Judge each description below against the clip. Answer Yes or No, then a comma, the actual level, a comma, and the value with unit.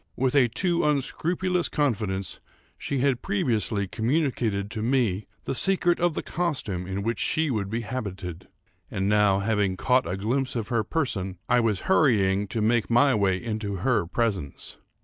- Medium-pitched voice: No, low, 115 Hz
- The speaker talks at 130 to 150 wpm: No, average, 165 wpm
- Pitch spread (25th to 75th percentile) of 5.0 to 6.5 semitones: Yes, wide, 5.5 semitones